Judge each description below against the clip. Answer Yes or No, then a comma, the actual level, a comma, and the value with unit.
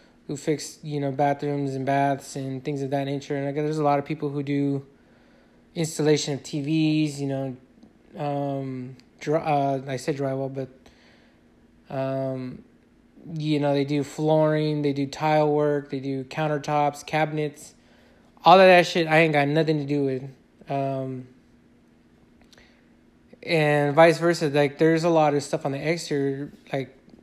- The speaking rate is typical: Yes, average, 160 wpm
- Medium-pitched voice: Yes, medium, 145 Hz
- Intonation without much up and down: Yes, narrow, 2.0 semitones